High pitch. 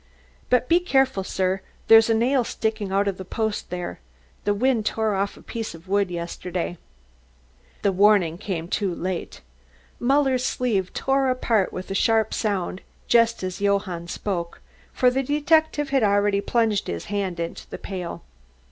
Yes: high, 205 Hz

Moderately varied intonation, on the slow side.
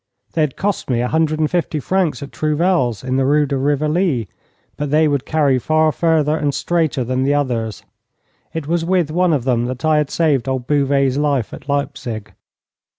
No: average, 3.1 semitones; average, 195 wpm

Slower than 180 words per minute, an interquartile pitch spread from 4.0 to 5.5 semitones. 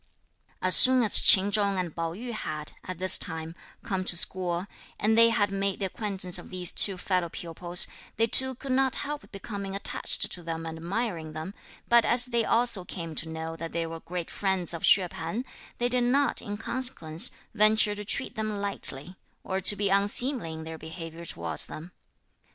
No: average, 190 wpm; average, 4.6 semitones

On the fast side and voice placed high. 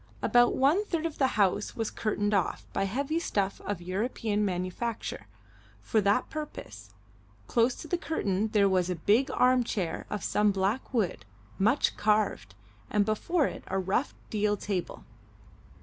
No: average, 155 wpm; high, 210 Hz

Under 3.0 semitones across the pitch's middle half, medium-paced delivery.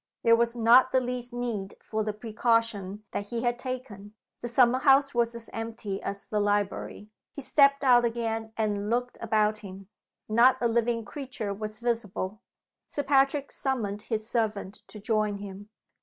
Yes: narrow, 2.6 semitones; average, 165 wpm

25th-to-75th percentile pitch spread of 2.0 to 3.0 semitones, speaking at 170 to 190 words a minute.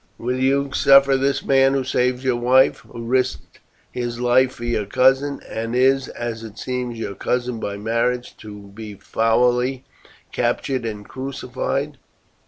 No: narrow, 2.4 semitones; average, 150 wpm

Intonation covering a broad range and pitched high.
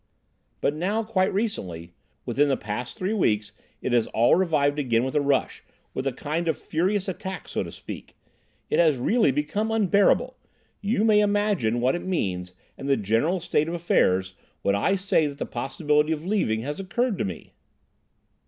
No: wide, 8.1 semitones; medium, 155 Hz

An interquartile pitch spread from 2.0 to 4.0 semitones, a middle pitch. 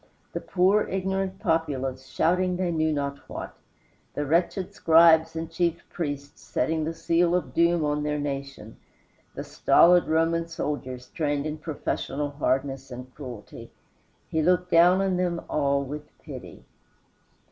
Yes: average, 3.4 semitones; medium, 160 Hz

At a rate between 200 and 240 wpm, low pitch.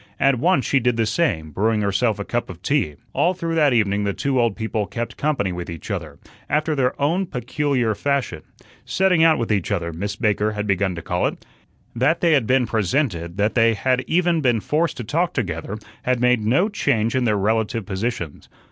Yes: fast, 205 wpm; low, 115 Hz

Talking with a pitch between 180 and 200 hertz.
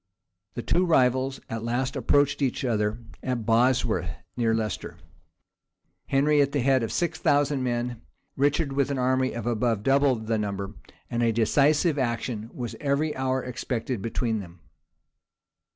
No: low, 125 Hz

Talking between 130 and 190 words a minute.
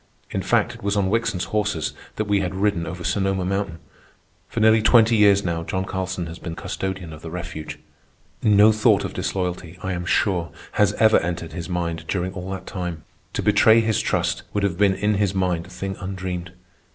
No: average, 200 wpm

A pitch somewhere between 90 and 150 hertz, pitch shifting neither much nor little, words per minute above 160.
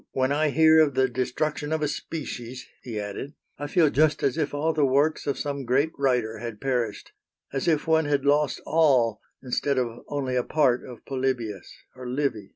Yes: low, 135 Hz; average, 3.2 semitones; average, 190 wpm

